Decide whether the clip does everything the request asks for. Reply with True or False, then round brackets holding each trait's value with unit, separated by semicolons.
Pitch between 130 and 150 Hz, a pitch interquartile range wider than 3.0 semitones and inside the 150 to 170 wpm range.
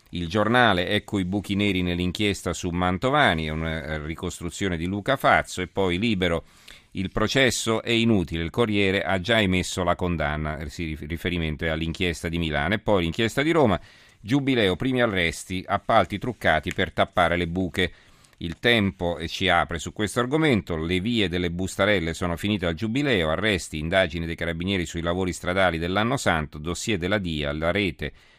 False (90 Hz; 3.8 semitones; 165 wpm)